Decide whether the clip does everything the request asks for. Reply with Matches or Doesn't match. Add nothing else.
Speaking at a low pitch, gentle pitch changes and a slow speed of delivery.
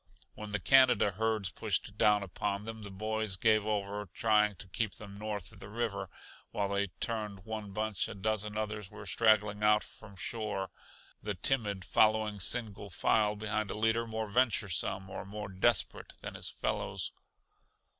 Doesn't match